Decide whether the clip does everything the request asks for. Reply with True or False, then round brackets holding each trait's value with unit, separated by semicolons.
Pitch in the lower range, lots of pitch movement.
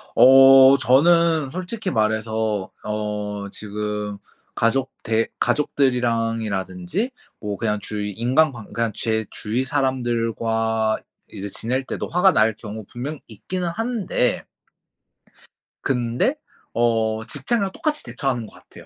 False (115 Hz; 4.0 semitones)